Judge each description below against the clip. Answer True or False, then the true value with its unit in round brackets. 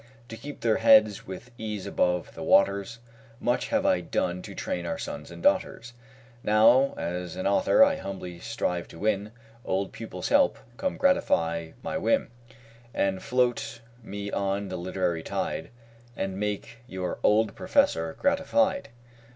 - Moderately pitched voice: False (100 Hz)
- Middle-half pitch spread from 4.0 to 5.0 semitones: True (4.4 semitones)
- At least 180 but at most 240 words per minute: False (150 wpm)